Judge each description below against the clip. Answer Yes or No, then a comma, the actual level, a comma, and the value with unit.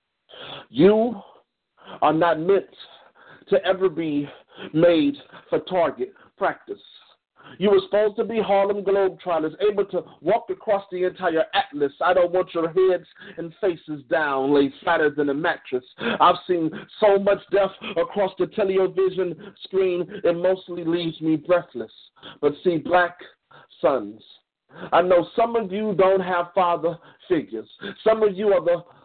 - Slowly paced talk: No, average, 145 wpm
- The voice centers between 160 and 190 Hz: Yes, medium, 185 Hz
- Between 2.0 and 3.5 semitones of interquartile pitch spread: Yes, average, 3.1 semitones